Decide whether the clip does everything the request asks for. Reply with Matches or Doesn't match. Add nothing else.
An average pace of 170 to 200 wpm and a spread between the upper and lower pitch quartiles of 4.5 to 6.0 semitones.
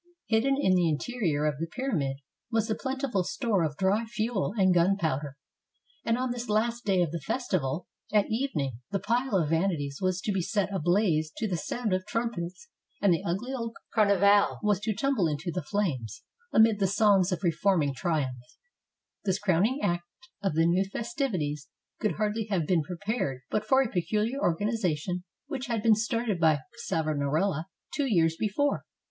Matches